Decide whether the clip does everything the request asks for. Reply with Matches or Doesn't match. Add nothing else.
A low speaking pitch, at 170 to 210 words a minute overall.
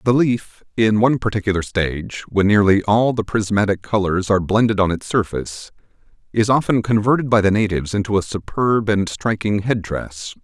Matches